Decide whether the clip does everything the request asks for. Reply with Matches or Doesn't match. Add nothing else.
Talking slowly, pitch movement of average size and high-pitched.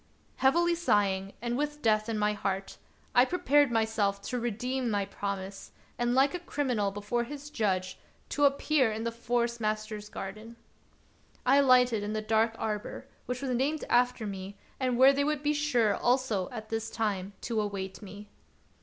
Doesn't match